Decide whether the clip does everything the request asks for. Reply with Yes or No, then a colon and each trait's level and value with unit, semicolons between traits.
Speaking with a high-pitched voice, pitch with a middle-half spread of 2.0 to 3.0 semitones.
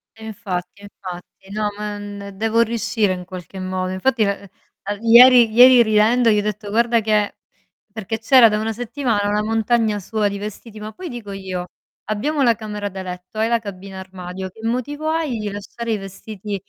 Yes: high, 210 Hz; average, 2.7 semitones